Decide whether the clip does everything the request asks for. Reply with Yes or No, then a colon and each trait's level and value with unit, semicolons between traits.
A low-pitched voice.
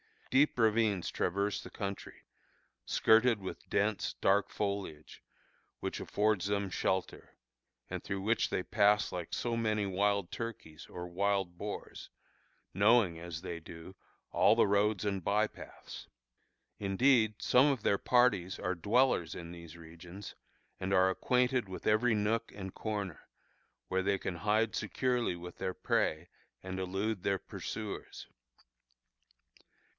Yes: low, 100 Hz